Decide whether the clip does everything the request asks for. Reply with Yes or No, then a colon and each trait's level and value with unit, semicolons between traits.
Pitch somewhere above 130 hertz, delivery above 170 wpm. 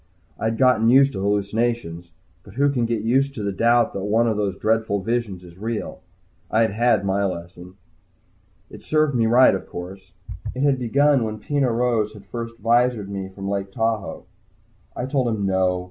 No: low, 110 Hz; average, 185 wpm